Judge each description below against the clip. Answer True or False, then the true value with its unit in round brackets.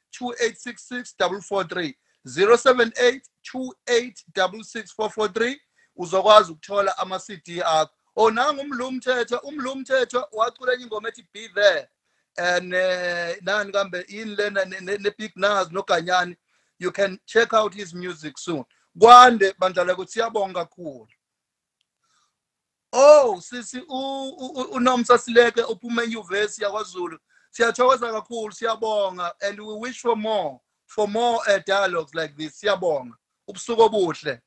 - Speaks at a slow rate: True (95 wpm)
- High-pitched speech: True (215 Hz)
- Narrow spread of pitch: False (4.5 semitones)